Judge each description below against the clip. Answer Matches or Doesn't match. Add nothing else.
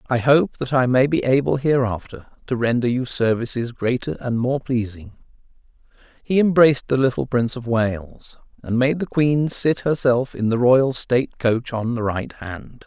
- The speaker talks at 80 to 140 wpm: Doesn't match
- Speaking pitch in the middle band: Doesn't match